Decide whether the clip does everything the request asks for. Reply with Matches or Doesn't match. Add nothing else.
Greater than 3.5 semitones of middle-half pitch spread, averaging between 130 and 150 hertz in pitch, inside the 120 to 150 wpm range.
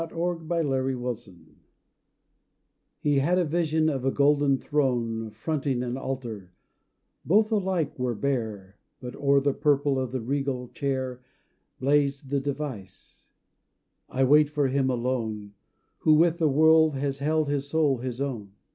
Doesn't match